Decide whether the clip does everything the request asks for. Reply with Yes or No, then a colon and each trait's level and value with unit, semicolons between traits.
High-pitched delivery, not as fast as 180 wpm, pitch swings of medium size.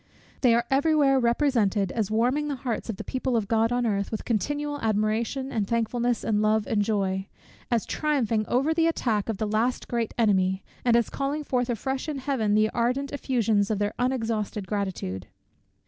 No: high, 230 Hz; average, 185 wpm; average, 3.7 semitones